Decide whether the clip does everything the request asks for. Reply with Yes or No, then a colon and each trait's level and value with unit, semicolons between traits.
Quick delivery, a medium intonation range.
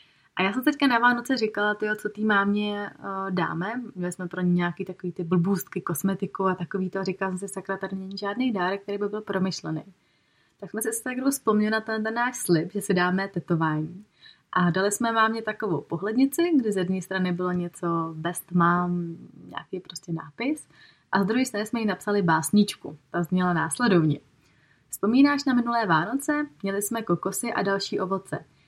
Yes: fast, 185 wpm; average, 3.6 semitones